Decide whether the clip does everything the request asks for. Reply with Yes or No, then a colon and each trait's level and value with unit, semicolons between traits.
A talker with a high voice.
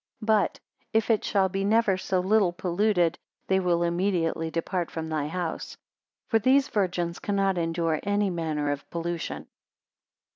No: medium, 180 Hz